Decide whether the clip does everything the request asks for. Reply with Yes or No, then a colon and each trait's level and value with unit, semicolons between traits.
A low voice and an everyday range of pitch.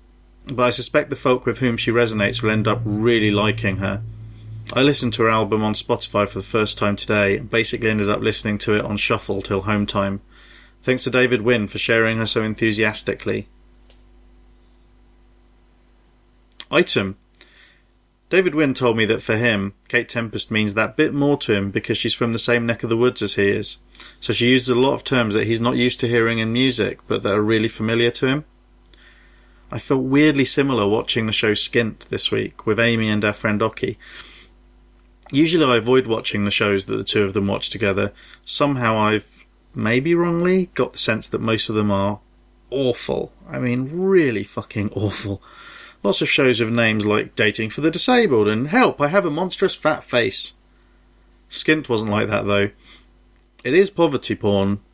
Yes: low, 110 Hz; average, 3.2 semitones